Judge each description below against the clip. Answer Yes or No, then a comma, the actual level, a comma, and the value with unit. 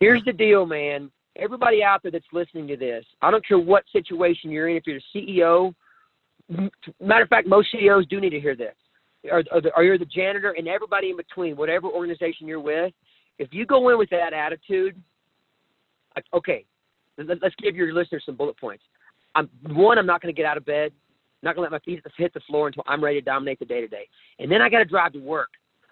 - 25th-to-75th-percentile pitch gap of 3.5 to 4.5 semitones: Yes, average, 4.1 semitones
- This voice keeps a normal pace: No, fast, 220 wpm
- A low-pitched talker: No, medium, 175 Hz